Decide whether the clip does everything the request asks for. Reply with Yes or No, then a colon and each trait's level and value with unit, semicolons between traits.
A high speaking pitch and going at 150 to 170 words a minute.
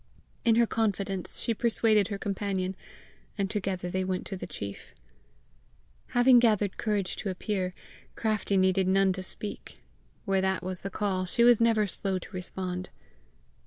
Yes: high, 195 Hz; average, 155 wpm